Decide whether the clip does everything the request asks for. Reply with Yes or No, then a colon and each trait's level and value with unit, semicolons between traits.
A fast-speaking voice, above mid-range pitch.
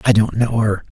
No: fast, 245 wpm; low, 105 Hz